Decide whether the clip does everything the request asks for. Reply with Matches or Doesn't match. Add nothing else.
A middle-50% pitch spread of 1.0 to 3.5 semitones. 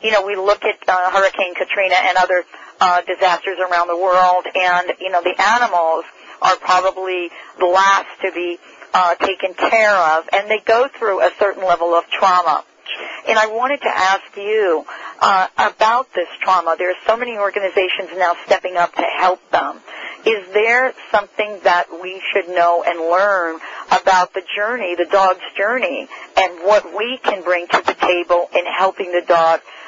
Matches